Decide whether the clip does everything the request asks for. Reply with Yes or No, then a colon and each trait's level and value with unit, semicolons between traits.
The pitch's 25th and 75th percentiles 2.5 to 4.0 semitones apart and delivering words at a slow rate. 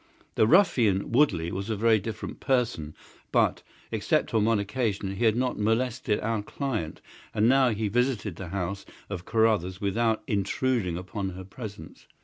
No: average, 3.5 semitones; average, 155 wpm